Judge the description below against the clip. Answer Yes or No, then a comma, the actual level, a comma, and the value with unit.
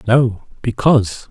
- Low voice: Yes, low, 120 Hz